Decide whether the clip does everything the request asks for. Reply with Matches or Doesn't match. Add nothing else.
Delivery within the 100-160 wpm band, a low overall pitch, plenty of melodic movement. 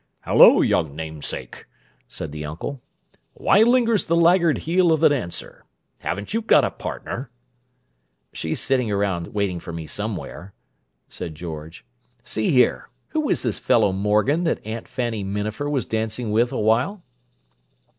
Matches